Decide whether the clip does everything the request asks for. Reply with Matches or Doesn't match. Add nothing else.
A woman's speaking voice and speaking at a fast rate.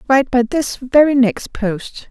Doesn't match